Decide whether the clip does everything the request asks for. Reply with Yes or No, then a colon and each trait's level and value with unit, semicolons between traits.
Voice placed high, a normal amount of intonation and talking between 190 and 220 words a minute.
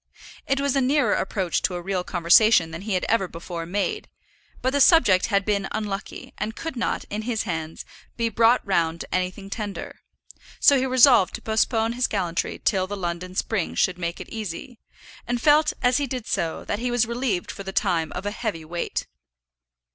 Yes: high, 205 Hz; average, 4.9 semitones; average, 195 wpm